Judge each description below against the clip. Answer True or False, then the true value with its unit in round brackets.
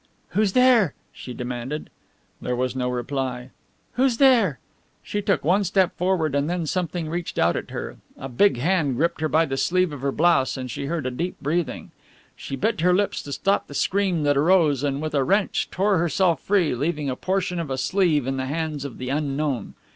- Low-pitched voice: False (155 Hz)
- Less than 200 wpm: False (205 wpm)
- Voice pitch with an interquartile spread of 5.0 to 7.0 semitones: True (5.4 semitones)